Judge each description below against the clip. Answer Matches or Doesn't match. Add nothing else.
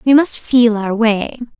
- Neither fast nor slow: Matches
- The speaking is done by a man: Doesn't match